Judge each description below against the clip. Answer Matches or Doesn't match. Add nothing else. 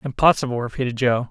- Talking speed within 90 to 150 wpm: Matches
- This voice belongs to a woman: Doesn't match